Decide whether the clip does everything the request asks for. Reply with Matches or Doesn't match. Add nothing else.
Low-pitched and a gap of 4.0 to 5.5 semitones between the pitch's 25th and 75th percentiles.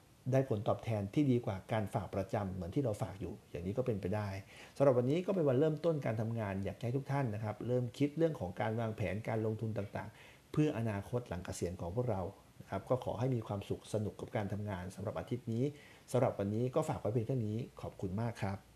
Matches